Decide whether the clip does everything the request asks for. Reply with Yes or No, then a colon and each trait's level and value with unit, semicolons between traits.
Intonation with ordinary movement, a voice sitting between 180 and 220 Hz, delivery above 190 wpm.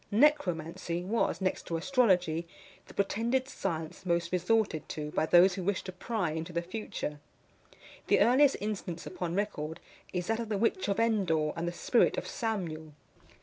No: average, 4.7 semitones; medium, 185 Hz; average, 165 wpm